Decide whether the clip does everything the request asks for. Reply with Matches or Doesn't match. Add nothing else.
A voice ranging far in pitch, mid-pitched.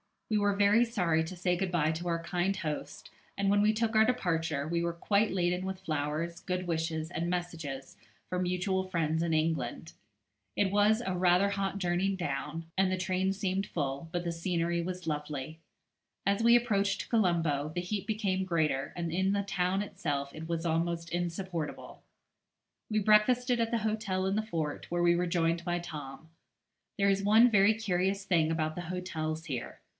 Doesn't match